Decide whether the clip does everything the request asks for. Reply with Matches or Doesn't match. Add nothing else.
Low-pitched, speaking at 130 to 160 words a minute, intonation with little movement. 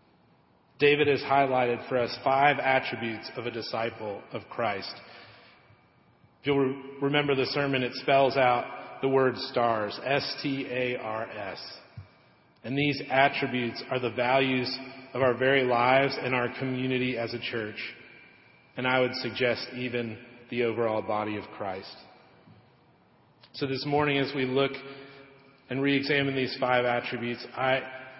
Matches